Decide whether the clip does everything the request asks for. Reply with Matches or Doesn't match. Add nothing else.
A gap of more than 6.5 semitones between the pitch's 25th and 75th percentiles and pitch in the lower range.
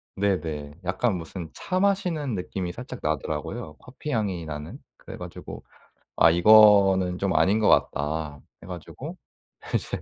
Doesn't match